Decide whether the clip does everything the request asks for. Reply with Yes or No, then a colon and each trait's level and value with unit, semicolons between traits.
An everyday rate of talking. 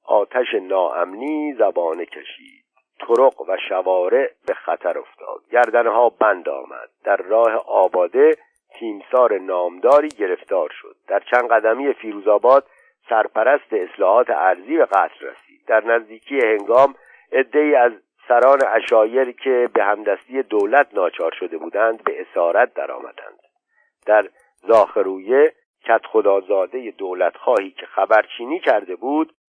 Yes: average, 115 wpm